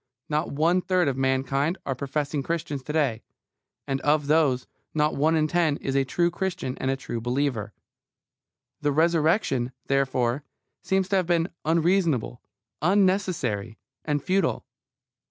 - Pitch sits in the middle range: Yes, medium, 150 Hz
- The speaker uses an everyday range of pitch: Yes, average, 4.2 semitones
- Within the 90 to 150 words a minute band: Yes, average, 140 wpm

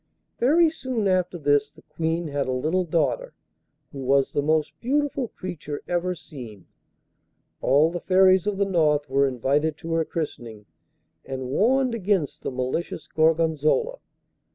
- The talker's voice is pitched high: No, medium, 160 Hz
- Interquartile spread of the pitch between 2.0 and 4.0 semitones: No, average, 4.8 semitones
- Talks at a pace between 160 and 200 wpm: No, average, 145 wpm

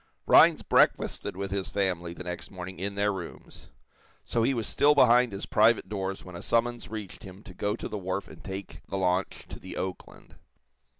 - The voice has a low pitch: Yes, low, 100 Hz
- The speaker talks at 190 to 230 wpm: Yes, average, 195 wpm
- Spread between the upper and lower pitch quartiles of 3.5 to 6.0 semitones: No, average, 2.7 semitones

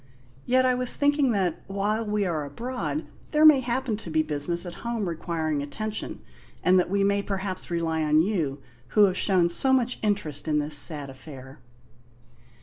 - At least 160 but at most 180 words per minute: Yes, average, 175 wpm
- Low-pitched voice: No, high, 190 Hz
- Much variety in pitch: Yes, wide, 6.2 semitones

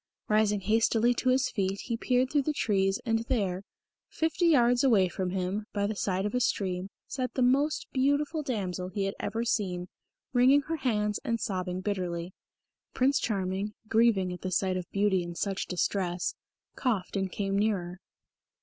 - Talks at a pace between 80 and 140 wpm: No, average, 170 wpm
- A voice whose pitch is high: Yes, high, 205 Hz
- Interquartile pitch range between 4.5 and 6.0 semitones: Yes, average, 4.8 semitones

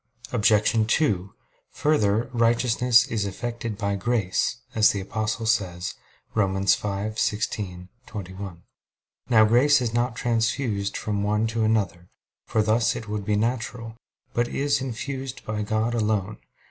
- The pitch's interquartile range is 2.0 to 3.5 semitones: Yes, average, 2.7 semitones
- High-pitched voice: No, low, 110 Hz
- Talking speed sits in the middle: No, slow, 130 wpm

